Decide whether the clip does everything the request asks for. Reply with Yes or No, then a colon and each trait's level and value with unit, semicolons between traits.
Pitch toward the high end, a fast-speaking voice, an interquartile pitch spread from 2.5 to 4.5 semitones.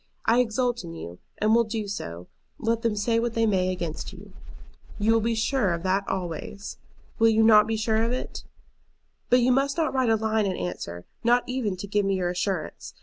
Yes: high, 220 Hz; fast, 210 wpm; average, 3.7 semitones